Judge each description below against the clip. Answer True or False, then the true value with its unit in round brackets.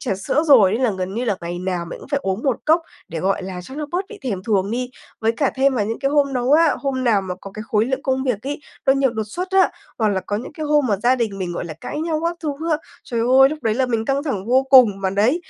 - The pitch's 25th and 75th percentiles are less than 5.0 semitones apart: False (5.6 semitones)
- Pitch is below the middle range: False (245 Hz)